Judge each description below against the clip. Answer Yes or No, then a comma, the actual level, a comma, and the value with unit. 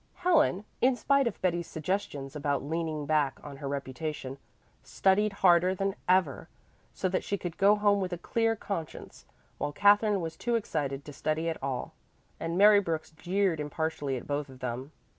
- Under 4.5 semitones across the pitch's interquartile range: No, wide, 5.4 semitones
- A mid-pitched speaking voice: Yes, medium, 165 Hz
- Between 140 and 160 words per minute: No, average, 175 wpm